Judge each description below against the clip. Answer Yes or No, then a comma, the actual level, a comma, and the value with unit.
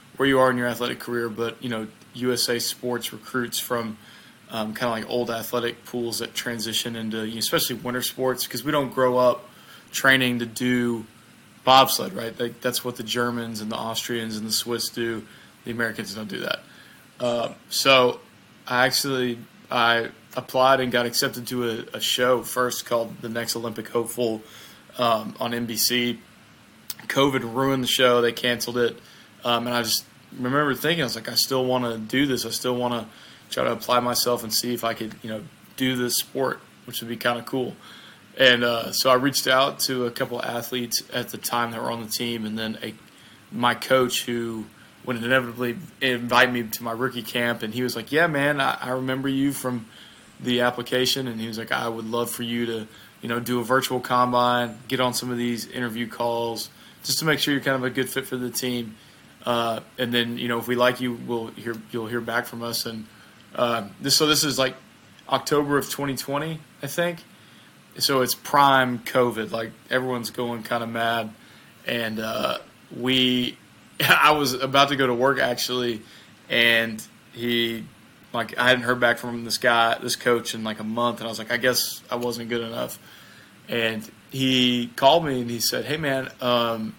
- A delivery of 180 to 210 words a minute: Yes, average, 200 wpm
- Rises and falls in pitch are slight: Yes, narrow, 1.6 semitones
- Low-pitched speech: Yes, low, 120 Hz